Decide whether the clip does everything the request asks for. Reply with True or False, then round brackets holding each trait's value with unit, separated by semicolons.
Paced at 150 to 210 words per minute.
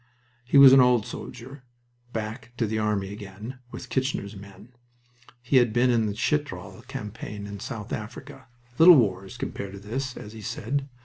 True (170 wpm)